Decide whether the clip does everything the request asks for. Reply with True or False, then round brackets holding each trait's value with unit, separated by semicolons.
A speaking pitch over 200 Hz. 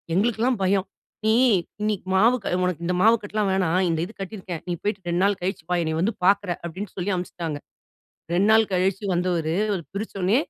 False (190 Hz)